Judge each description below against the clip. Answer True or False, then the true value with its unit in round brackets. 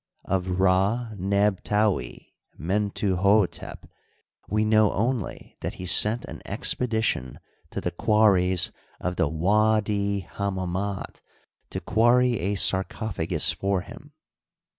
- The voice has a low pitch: True (100 Hz)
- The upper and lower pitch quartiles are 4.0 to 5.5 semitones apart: False (2.7 semitones)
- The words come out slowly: True (105 wpm)